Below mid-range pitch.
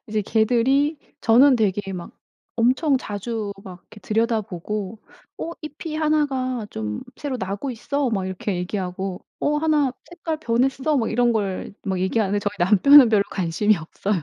No: high, 225 Hz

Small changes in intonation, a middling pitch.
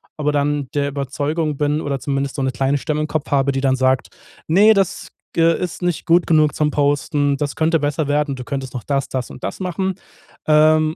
Yes: narrow, 2.3 semitones; medium, 145 Hz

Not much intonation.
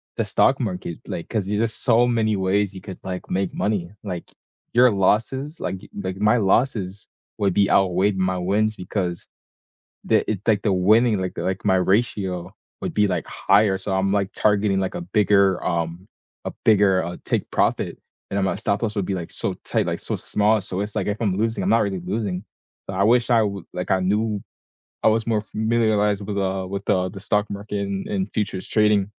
Yes: narrow, 2.3 semitones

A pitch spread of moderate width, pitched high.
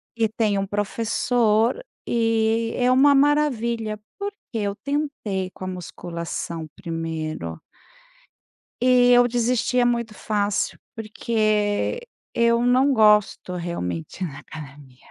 Yes: average, 4.7 semitones; high, 220 Hz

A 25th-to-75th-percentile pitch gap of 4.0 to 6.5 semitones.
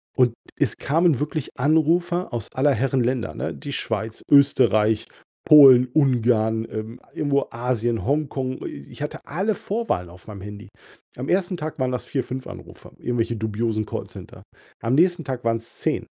Yes: average, 4.7 semitones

